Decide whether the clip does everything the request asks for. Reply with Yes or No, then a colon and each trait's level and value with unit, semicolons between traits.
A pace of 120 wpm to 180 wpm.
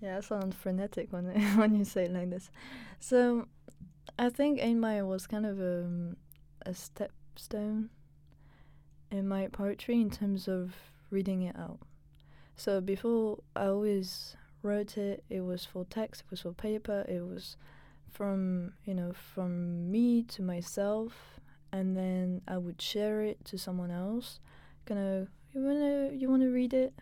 Yes: average, 160 wpm